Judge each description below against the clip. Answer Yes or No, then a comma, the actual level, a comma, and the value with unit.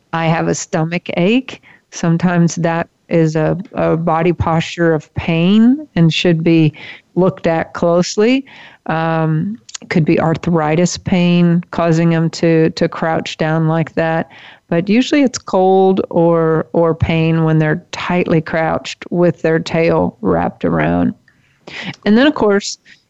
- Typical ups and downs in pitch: No, narrow, 2.0 semitones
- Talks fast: No, average, 140 wpm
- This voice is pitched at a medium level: Yes, medium, 170 Hz